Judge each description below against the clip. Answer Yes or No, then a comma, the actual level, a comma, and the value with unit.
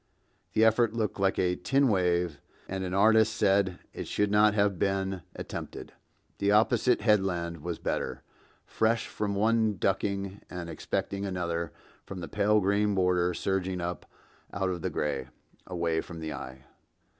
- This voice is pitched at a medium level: No, very low, 95 Hz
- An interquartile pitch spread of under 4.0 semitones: Yes, average, 2.9 semitones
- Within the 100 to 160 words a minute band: Yes, average, 155 wpm